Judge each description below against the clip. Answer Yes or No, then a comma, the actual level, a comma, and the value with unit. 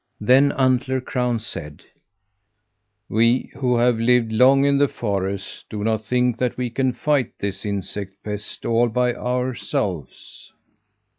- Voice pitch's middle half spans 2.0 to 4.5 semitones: Yes, average, 3.4 semitones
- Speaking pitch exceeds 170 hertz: No, low, 120 Hz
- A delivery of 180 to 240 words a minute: No, slow, 135 wpm